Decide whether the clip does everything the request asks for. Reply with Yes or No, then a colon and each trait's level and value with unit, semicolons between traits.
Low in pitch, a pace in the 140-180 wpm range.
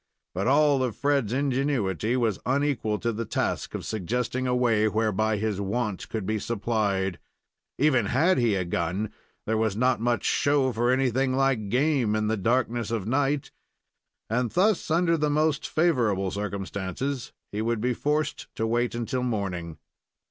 Yes: low, 120 Hz; average, 160 wpm